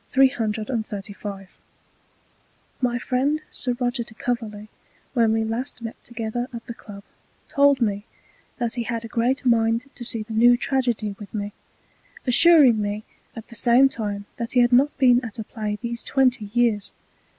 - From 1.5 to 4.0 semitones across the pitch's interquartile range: Yes, narrow, 2.4 semitones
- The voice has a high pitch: Yes, high, 235 Hz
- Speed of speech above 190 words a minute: No, average, 160 wpm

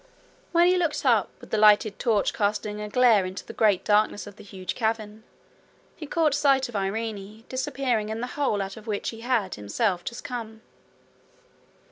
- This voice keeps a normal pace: Yes, average, 180 wpm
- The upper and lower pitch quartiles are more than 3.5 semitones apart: No, average, 3.2 semitones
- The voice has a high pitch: Yes, high, 220 Hz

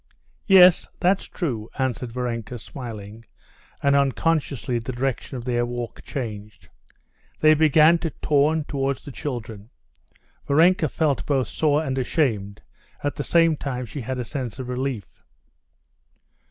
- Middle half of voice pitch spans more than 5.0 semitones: No, average, 4.1 semitones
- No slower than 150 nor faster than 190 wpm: No, slow, 135 wpm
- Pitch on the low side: Yes, low, 130 Hz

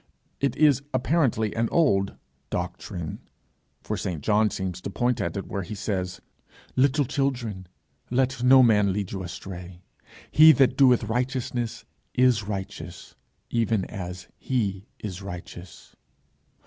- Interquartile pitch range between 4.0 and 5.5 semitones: Yes, average, 5.1 semitones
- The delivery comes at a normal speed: No, slow, 130 wpm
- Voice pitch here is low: Yes, low, 110 Hz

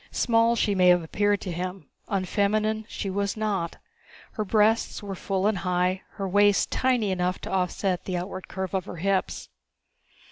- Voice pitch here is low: No, high, 195 Hz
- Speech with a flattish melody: Yes, narrow, 2.3 semitones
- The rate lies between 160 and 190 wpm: Yes, average, 170 wpm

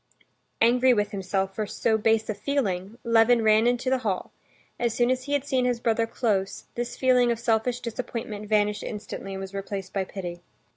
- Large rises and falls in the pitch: No, average, 3.3 semitones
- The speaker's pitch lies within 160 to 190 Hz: No, high, 225 Hz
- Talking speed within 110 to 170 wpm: No, average, 190 wpm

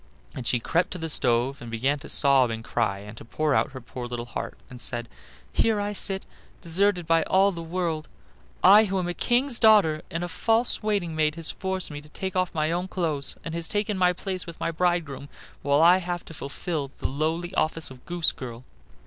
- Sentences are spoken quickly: Yes, fast, 215 wpm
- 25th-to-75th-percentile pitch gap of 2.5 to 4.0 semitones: No, average, 4.8 semitones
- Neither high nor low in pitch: Yes, medium, 165 Hz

